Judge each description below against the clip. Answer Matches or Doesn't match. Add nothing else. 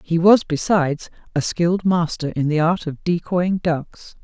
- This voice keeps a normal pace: Matches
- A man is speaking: Doesn't match